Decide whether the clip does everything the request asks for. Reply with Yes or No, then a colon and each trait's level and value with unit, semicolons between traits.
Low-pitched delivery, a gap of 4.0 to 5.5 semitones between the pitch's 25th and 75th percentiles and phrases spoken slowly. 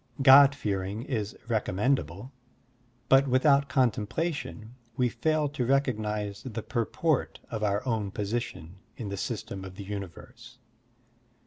Yes: low, 115 Hz; average, 4.6 semitones; slow, 125 wpm